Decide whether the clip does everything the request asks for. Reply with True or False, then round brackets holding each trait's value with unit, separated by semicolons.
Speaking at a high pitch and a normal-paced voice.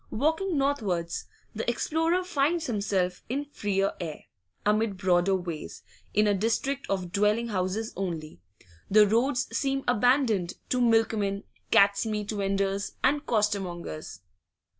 False (210 Hz; 120 wpm)